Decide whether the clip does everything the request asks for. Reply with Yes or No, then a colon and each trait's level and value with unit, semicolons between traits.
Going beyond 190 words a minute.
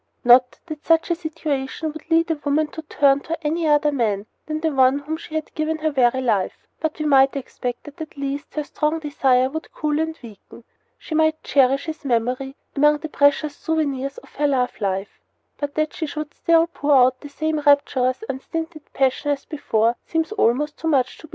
Yes: fast, 205 wpm